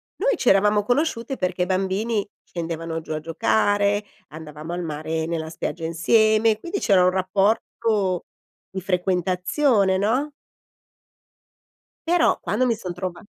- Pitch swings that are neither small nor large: Yes, average, 4.2 semitones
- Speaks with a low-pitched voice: No, high, 190 Hz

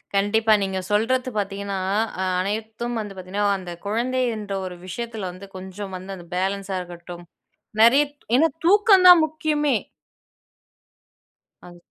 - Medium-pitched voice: No, high, 205 Hz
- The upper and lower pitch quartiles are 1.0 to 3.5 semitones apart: No, average, 4.2 semitones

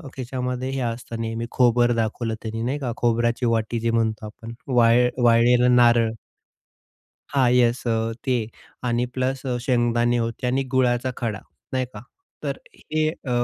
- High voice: No, low, 120 Hz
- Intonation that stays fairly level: Yes, narrow, 1.5 semitones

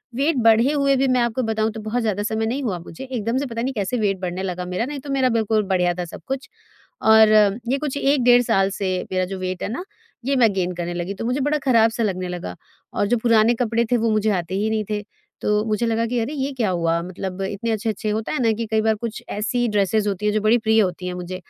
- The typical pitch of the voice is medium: No, high, 220 Hz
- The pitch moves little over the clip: No, average, 4.0 semitones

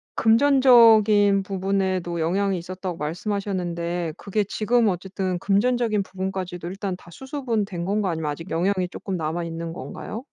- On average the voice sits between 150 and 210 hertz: Yes, high, 190 Hz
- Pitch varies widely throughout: No, average, 3.2 semitones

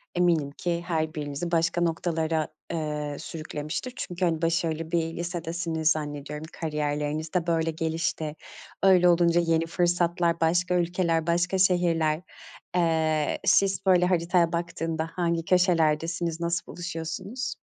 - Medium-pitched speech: Yes, medium, 165 Hz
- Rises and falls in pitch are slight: Yes, narrow, 1.6 semitones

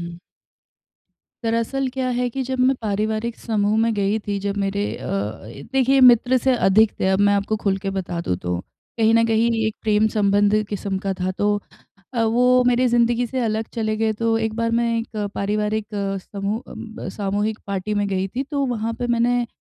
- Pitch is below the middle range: No, high, 220 Hz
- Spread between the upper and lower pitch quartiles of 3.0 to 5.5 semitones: No, narrow, 2.6 semitones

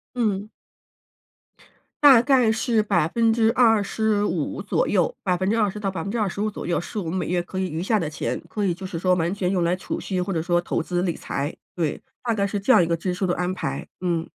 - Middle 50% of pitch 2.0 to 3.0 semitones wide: No, average, 3.7 semitones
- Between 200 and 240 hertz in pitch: No, high, 190 Hz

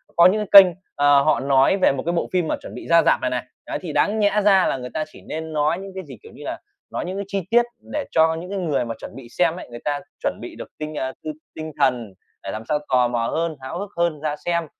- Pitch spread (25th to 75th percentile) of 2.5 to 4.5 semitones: No, average, 5.2 semitones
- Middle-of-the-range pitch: Yes, medium, 160 Hz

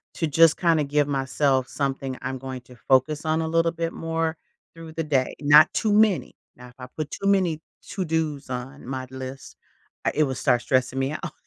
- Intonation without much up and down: No, average, 3.7 semitones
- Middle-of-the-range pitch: Yes, medium, 145 Hz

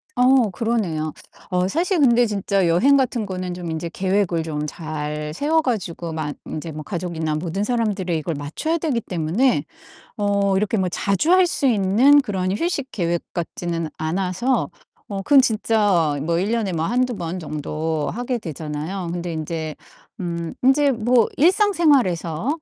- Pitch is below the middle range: No, high, 190 Hz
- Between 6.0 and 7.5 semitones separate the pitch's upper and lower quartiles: Yes, wide, 6.6 semitones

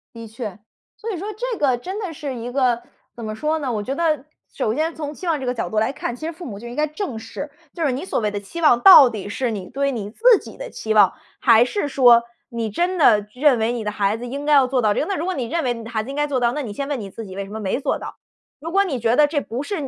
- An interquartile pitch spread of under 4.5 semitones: No, average, 5.2 semitones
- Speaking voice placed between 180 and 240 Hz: No, very high, 255 Hz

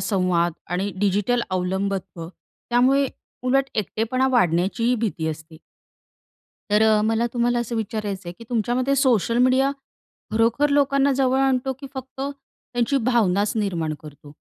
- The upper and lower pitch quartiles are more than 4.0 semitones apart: Yes, average, 5.1 semitones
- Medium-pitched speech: No, high, 230 Hz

